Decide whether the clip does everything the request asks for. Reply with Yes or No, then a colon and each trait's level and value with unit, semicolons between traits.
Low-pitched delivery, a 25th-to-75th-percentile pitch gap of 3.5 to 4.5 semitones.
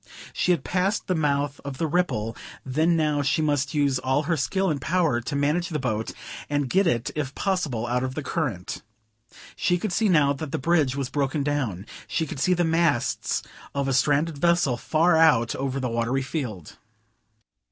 No: medium, 145 Hz; average, 4.0 semitones